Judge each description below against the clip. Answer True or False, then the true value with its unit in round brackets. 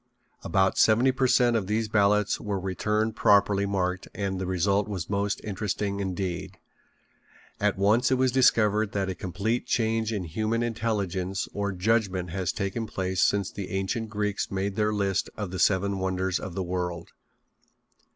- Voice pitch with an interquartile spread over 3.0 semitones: False (2.4 semitones)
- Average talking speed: True (160 wpm)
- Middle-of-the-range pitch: False (100 Hz)